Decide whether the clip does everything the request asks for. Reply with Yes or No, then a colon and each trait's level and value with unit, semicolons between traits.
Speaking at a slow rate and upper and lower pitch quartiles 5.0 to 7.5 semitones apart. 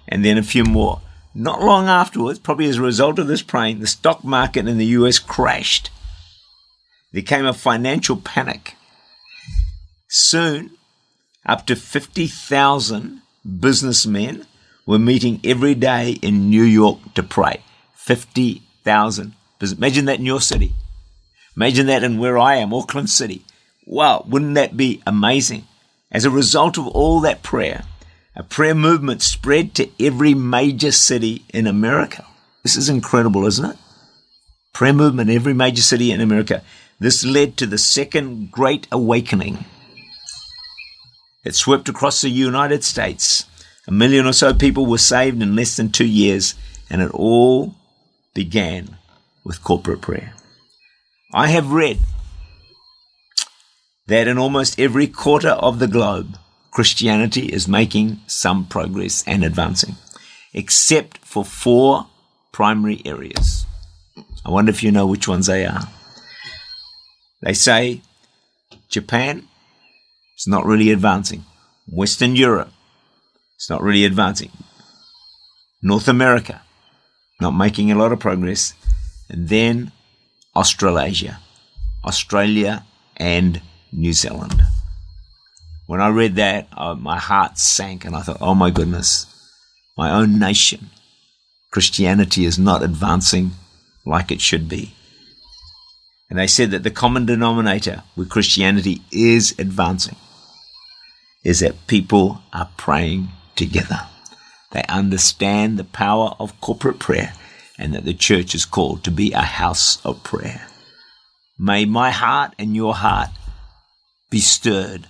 Yes: slow, 130 wpm; wide, 5.5 semitones